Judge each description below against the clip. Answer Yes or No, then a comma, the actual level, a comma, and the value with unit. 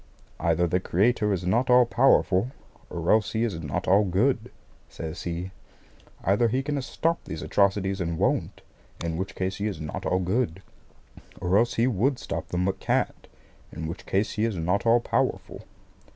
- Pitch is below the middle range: Yes, low, 100 Hz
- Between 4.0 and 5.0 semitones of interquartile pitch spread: Yes, average, 4.7 semitones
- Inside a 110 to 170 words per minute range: No, average, 180 wpm